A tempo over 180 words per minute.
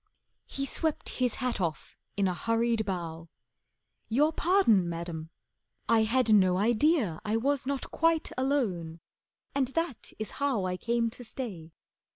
No: average, 145 wpm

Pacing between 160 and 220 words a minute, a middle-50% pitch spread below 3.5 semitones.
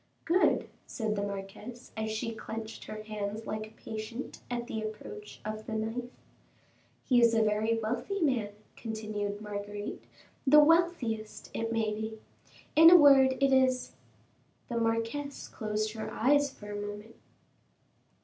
No: average, 150 wpm; average, 2.9 semitones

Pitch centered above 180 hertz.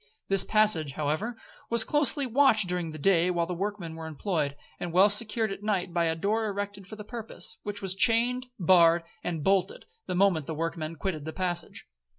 Yes: high, 190 Hz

